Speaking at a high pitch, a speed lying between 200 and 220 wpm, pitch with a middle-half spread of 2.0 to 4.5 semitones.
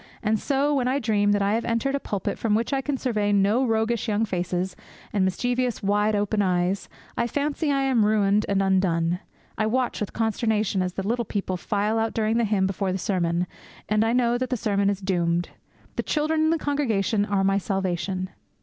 Yes: high, 210 Hz; fast, 205 wpm; average, 3.5 semitones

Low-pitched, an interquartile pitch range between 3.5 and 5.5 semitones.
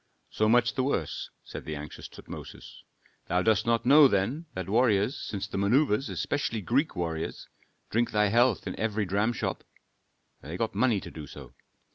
Yes: low, 110 Hz; average, 3.9 semitones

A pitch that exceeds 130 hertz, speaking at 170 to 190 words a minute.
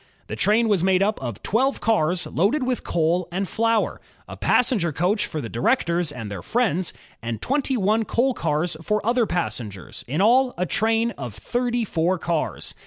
Yes: high, 190 Hz; average, 175 wpm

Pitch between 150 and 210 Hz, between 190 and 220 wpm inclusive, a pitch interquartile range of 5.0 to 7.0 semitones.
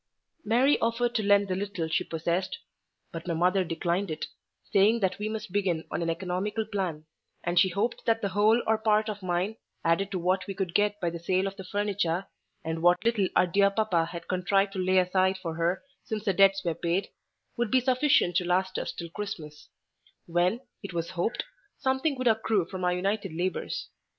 No: high, 190 Hz; average, 200 wpm; average, 3.1 semitones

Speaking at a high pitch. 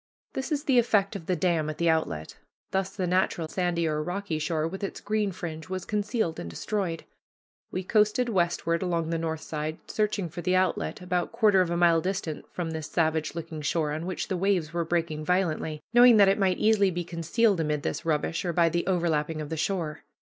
No: medium, 175 Hz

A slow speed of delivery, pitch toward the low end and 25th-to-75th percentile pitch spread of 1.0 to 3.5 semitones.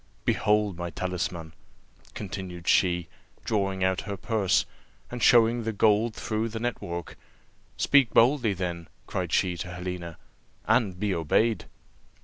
No: slow, 130 wpm; very low, 95 Hz; average, 4.0 semitones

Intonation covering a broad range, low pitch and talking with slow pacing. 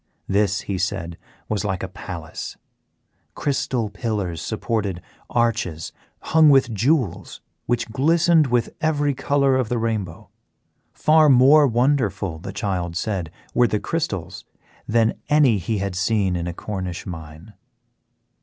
Yes: wide, 6.0 semitones; low, 110 Hz; slow, 130 wpm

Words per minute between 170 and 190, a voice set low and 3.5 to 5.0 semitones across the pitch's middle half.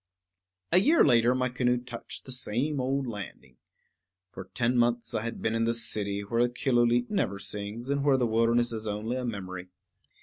No: average, 180 wpm; low, 120 Hz; average, 2.8 semitones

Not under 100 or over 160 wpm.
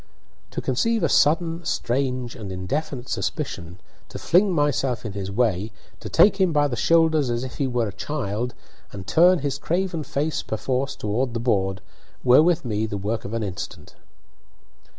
No: average, 170 wpm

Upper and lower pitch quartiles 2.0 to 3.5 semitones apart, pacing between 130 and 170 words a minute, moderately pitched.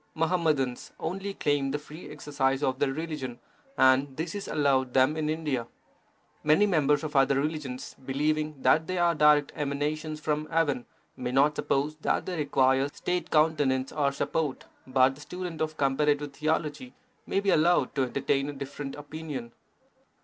Yes: narrow, 2.5 semitones; average, 155 wpm; medium, 150 Hz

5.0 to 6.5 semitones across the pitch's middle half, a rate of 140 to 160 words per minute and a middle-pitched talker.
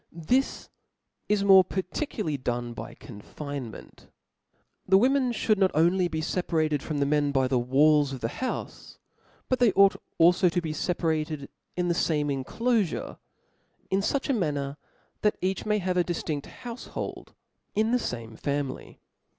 Yes: wide, 5.6 semitones; average, 150 wpm; medium, 165 Hz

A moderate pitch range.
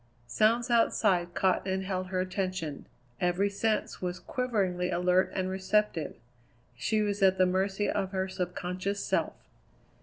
No: narrow, 2.0 semitones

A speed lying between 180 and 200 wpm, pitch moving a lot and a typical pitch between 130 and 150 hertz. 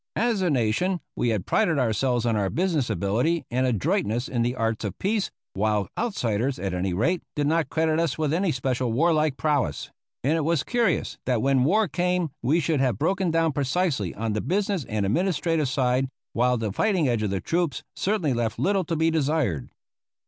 Yes: average, 190 wpm; wide, 6.4 semitones; medium, 140 Hz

